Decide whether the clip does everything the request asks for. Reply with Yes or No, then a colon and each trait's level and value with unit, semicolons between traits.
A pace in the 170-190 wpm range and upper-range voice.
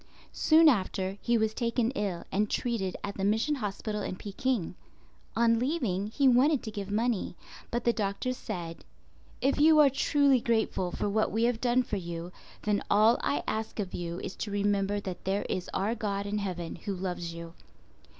Yes: average, 185 wpm; high, 210 Hz